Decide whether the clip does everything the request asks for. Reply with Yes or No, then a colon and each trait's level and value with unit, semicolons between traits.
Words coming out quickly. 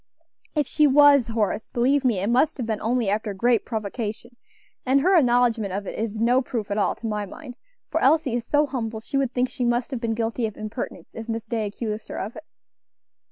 Yes: fast, 220 wpm